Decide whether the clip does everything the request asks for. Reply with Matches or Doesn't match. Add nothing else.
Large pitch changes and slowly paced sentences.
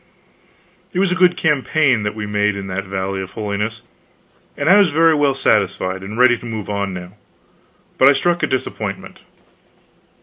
Doesn't match